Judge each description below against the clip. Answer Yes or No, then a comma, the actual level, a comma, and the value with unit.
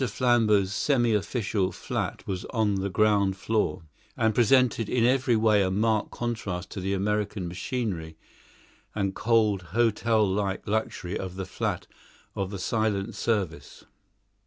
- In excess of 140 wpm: No, slow, 135 wpm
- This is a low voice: Yes, low, 105 Hz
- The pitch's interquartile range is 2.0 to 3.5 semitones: Yes, average, 2.8 semitones